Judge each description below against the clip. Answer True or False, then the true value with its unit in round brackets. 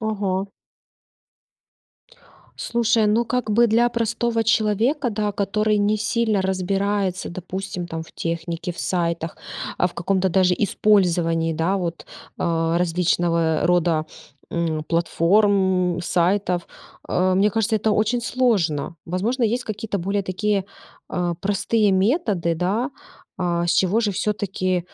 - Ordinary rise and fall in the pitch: True (3.6 semitones)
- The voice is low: False (190 Hz)